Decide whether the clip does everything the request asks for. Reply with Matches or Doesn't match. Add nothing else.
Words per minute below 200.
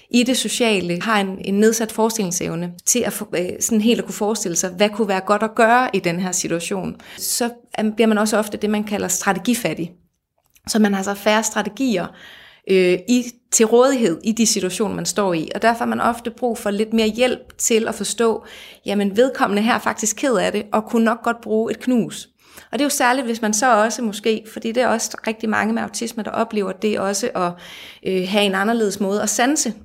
Doesn't match